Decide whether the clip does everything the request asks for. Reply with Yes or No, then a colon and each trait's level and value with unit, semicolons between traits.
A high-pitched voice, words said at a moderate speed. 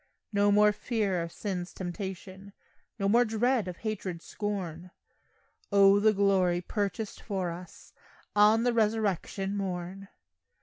No: high, 200 Hz; slow, 125 wpm